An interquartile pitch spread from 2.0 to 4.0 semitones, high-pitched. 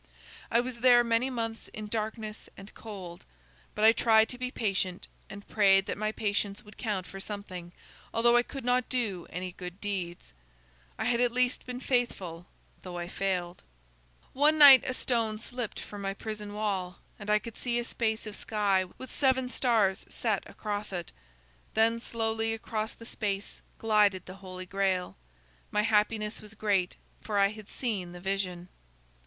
Yes: average, 3.1 semitones; high, 215 Hz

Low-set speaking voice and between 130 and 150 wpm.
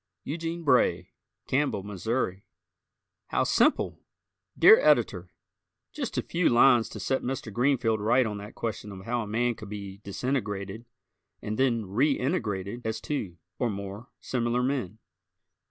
Yes: low, 115 Hz; average, 140 wpm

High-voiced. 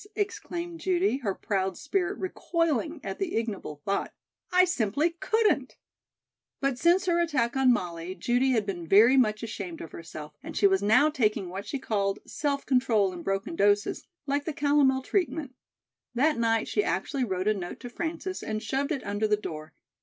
Yes: high, 245 Hz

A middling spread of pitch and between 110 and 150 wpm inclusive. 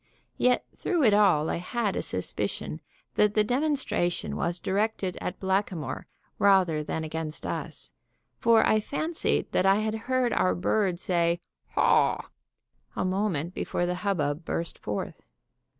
Yes: average, 4.2 semitones; average, 140 wpm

